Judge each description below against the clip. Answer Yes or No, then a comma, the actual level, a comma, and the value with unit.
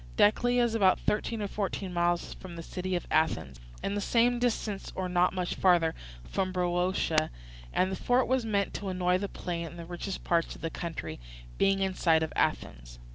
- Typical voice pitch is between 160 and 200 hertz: Yes, medium, 185 Hz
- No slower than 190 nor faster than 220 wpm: Yes, average, 195 wpm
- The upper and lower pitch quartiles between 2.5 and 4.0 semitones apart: Yes, average, 2.8 semitones